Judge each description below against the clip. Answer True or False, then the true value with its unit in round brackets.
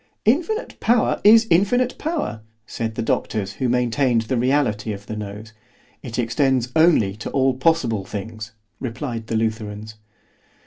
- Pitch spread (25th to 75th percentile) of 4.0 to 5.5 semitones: True (5.2 semitones)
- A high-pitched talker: False (120 Hz)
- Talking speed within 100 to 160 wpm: True (140 wpm)